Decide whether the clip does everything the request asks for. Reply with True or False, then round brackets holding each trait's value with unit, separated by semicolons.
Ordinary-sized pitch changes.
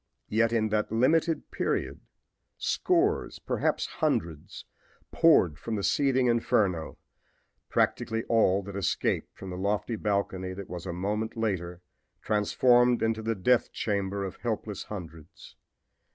True (3.6 semitones)